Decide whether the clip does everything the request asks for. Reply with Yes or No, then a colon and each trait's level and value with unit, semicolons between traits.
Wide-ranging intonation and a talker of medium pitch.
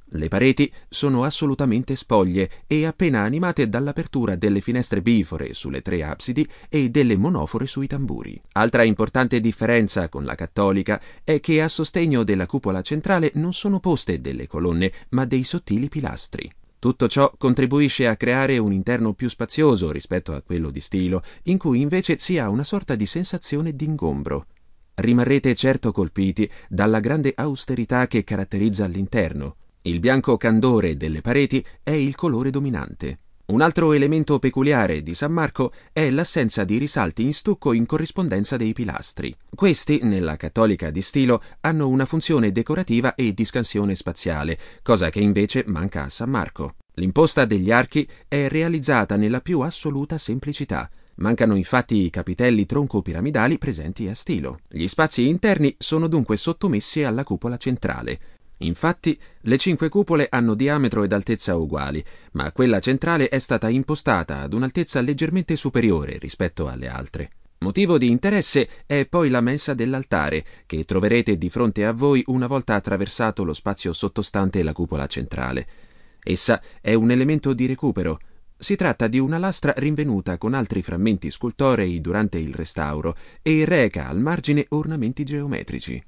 No: wide, 7.0 semitones; low, 120 Hz